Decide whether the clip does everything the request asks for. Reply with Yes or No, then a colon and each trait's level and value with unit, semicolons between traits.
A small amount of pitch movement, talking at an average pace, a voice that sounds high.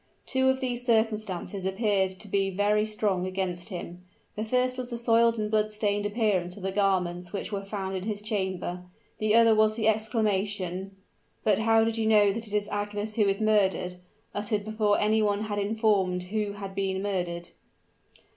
Yes: narrow, 2.2 semitones; average, 180 wpm; high, 205 Hz